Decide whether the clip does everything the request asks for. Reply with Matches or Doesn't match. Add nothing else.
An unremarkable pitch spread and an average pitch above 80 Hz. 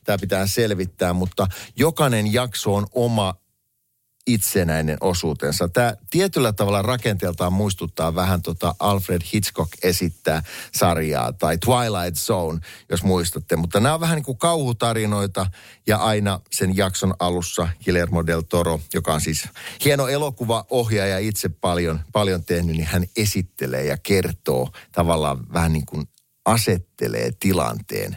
Matches